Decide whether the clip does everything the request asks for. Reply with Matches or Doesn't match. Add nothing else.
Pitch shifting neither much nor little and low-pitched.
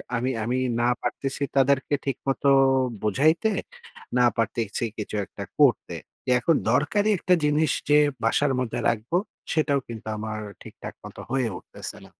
Matches